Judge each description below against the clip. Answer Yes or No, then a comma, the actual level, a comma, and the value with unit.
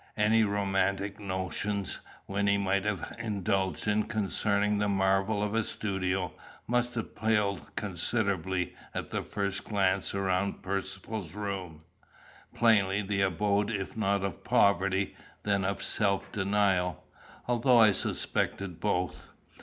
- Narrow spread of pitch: Yes, narrow, 1.5 semitones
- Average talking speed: No, slow, 120 wpm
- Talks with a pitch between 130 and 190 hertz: No, low, 100 Hz